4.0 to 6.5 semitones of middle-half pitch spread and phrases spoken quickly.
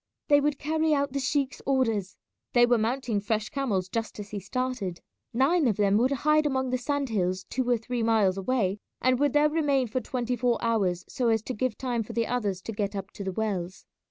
Yes: average, 4.4 semitones; fast, 220 wpm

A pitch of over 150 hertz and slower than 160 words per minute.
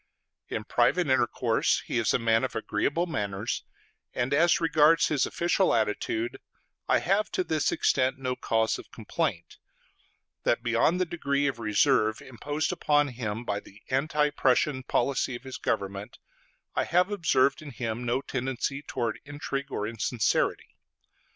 No: low, 130 Hz; average, 150 wpm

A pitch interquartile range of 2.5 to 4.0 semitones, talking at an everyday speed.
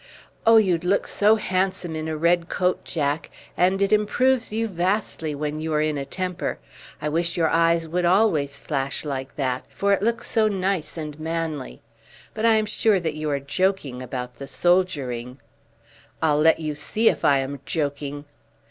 No: average, 4.7 semitones; average, 180 wpm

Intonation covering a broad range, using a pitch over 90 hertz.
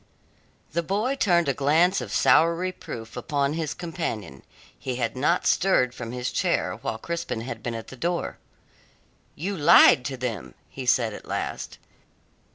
Yes: wide, 6.3 semitones; medium, 140 Hz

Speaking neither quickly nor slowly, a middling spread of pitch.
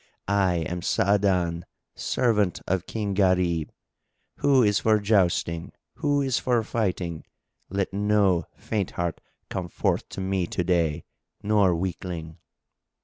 No: slow, 125 wpm; average, 3.2 semitones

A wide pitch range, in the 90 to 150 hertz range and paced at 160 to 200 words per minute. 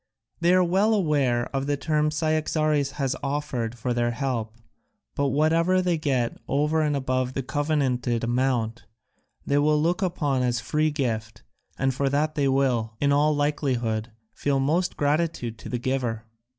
No: average, 3.7 semitones; medium, 140 Hz; average, 165 wpm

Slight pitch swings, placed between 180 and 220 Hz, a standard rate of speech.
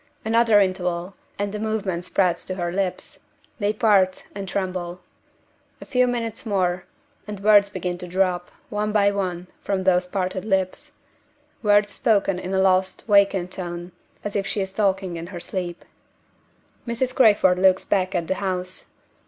Yes: narrow, 2.2 semitones; high, 190 Hz; average, 160 wpm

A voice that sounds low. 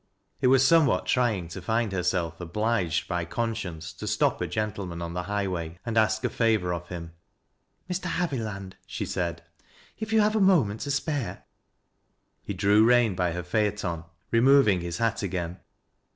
Yes: low, 100 Hz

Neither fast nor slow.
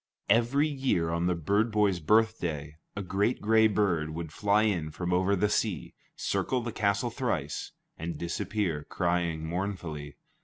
Yes: average, 150 wpm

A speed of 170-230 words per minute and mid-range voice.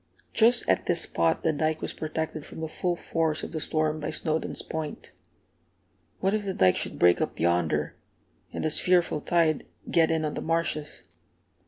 Yes: average, 180 wpm; medium, 155 Hz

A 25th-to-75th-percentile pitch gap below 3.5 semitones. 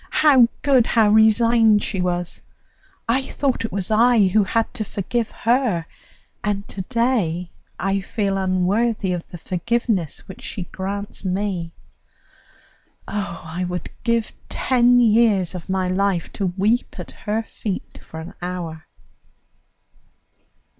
No: average, 4.1 semitones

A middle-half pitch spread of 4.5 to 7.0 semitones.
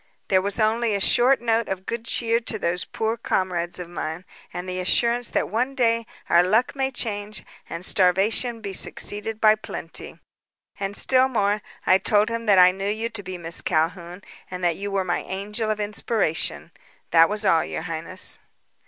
No: average, 3.7 semitones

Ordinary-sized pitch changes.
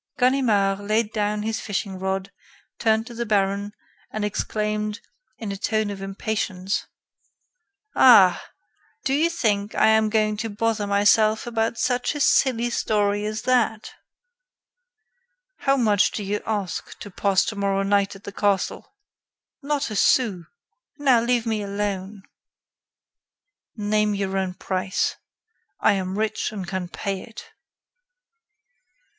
No: narrow, 2.0 semitones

